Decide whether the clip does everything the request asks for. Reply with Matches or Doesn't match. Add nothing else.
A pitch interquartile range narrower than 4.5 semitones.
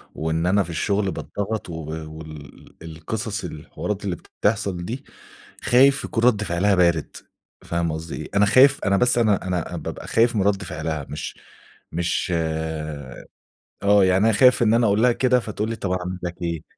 Doesn't match